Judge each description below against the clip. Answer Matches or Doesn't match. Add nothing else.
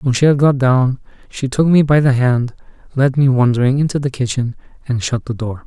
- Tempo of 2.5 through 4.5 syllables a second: Doesn't match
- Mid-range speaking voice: Doesn't match